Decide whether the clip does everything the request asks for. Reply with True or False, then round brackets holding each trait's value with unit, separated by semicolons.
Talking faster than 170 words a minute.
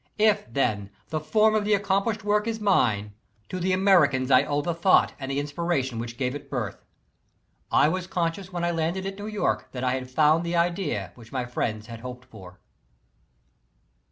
True (190 wpm)